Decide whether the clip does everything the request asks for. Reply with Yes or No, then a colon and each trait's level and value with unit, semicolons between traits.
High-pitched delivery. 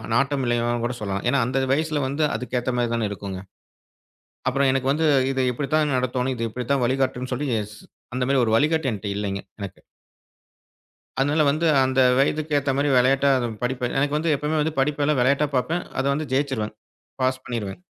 No: low, 135 Hz